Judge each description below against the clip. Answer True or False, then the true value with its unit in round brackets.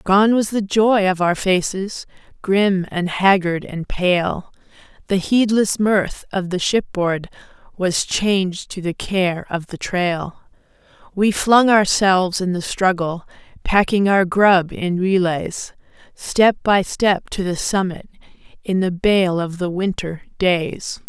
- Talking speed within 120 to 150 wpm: True (140 wpm)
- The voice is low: False (190 Hz)